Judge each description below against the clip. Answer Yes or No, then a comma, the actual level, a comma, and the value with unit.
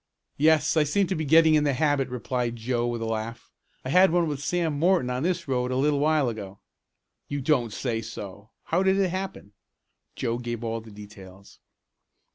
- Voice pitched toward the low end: Yes, low, 130 Hz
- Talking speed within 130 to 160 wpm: No, average, 190 wpm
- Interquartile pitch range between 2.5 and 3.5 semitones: No, wide, 5.6 semitones